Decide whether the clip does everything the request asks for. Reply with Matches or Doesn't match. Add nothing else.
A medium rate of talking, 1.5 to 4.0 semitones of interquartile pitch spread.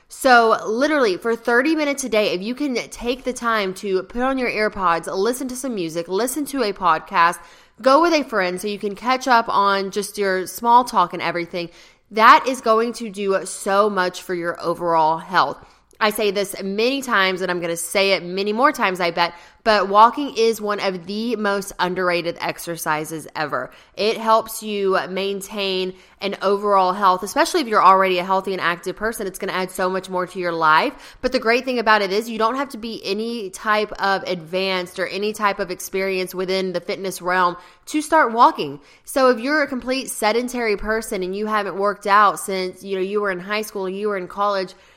Doesn't match